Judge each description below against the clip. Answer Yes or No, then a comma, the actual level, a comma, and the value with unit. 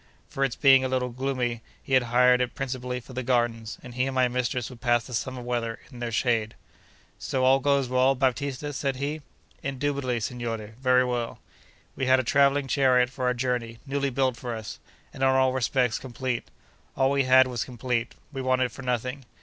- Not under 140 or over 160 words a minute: No, average, 200 wpm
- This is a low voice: Yes, low, 130 Hz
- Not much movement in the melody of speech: Yes, narrow, 1.6 semitones